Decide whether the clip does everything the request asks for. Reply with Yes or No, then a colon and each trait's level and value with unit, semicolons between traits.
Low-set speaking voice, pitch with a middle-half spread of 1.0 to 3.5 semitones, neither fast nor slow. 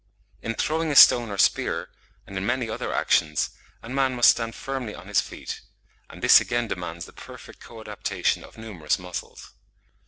No: low, 115 Hz; average, 4.5 semitones; average, 180 wpm